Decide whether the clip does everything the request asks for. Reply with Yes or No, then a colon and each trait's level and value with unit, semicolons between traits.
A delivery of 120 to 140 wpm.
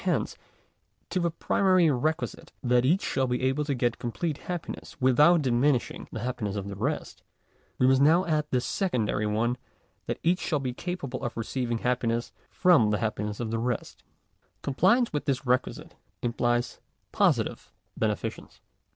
No: average, 160 wpm